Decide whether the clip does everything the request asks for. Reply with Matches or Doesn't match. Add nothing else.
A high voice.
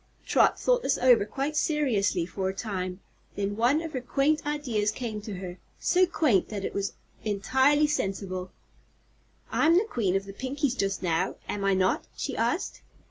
Matches